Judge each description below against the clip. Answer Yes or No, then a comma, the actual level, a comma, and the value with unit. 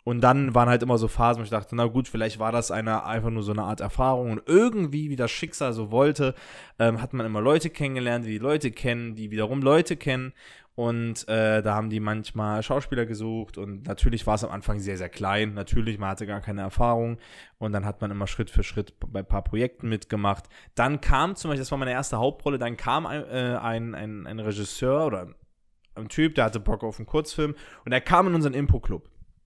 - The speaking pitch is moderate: No, low, 115 Hz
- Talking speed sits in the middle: No, fast, 230 wpm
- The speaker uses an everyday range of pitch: Yes, average, 3.7 semitones